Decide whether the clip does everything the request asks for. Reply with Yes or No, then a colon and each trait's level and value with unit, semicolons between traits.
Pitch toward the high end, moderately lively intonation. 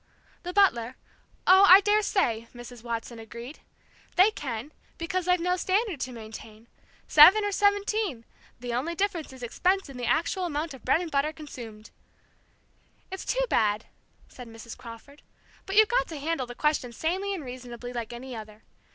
No: very high, 285 Hz; wide, 7.7 semitones